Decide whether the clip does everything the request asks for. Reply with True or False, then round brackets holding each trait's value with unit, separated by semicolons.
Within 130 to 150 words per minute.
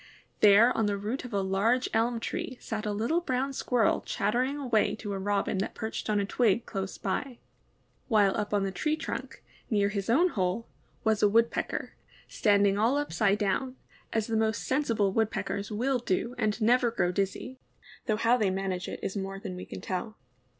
False (190 wpm)